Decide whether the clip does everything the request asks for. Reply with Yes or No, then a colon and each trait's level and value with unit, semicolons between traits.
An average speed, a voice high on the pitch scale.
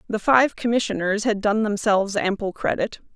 Yes: average, 150 wpm; high, 210 Hz